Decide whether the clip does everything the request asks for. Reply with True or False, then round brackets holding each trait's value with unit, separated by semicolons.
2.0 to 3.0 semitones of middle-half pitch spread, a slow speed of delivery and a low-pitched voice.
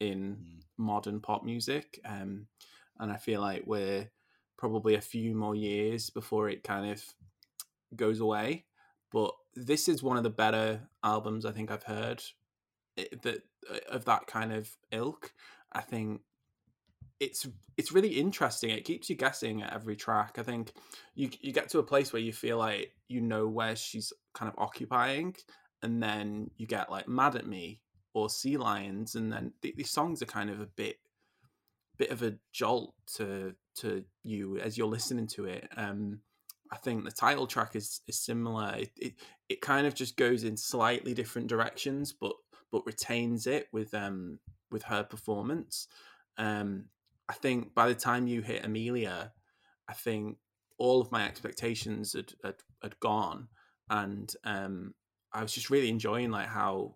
False (2.4 semitones; 170 wpm; 110 Hz)